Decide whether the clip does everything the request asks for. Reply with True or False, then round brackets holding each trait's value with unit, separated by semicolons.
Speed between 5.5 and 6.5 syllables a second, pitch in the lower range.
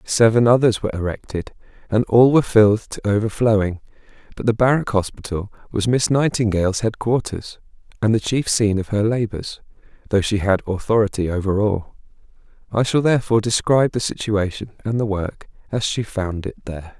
True (5.7 syllables/s; 110 Hz)